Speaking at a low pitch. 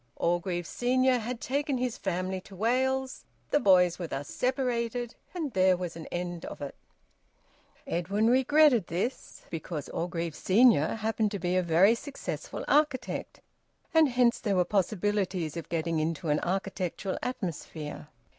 No: high, 195 Hz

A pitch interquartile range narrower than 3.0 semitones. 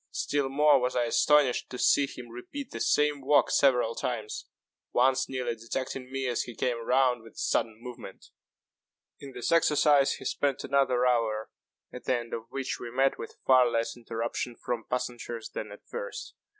Yes: narrow, 2.5 semitones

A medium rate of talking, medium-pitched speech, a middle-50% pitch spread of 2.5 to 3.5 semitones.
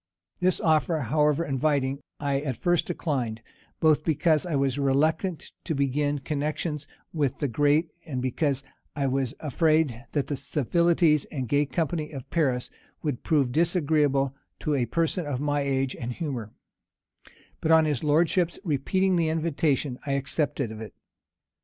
Yes: average, 150 wpm; medium, 145 Hz; average, 2.8 semitones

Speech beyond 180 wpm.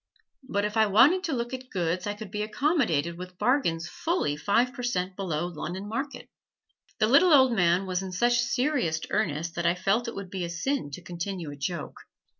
Yes: fast, 205 wpm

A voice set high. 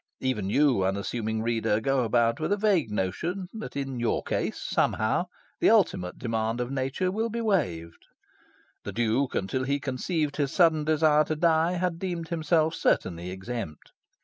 No: low, 135 Hz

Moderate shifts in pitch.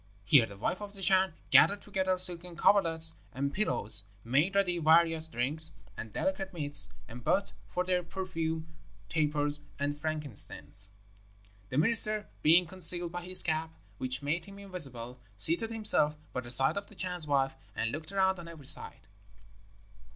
Yes: average, 4.5 semitones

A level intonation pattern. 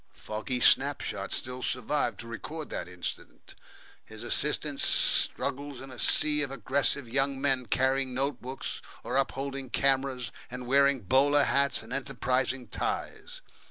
Yes: narrow, 1.7 semitones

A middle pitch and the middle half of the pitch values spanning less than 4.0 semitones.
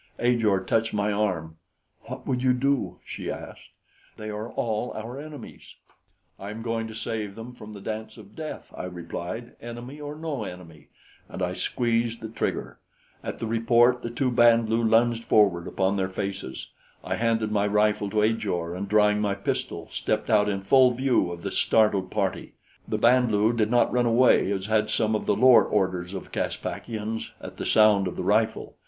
No: low, 110 Hz; average, 2.9 semitones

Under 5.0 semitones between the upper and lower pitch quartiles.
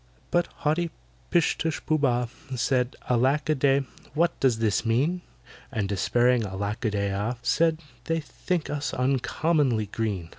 No: wide, 5.6 semitones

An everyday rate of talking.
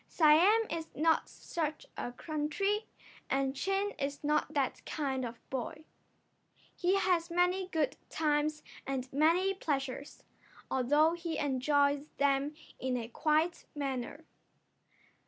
No: slow, 120 wpm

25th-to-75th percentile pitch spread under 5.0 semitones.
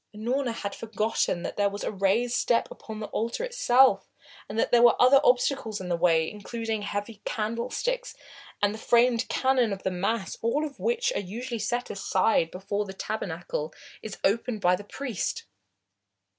Yes: average, 3.5 semitones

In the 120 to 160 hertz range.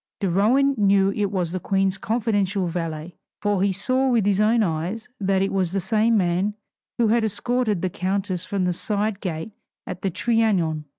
No: high, 195 Hz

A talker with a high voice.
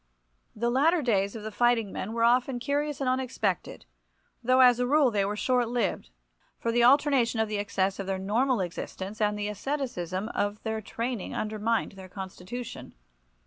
Yes: high, 230 Hz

